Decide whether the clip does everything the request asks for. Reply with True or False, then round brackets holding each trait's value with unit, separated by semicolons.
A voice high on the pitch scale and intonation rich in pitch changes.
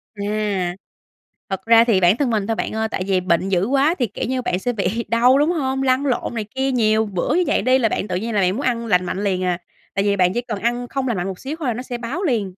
False (225 Hz; 4.7 semitones)